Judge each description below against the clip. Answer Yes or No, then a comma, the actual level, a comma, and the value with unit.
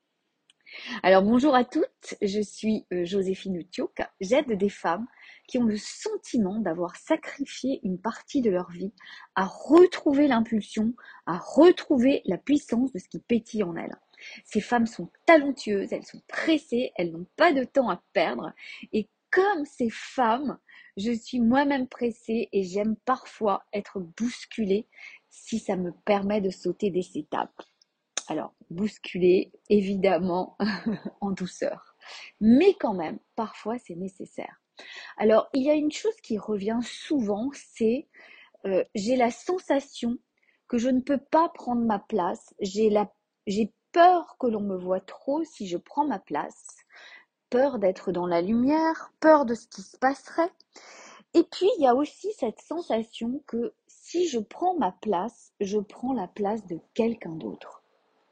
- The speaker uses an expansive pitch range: Yes, wide, 5.7 semitones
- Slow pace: No, average, 155 wpm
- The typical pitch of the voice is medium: No, high, 230 Hz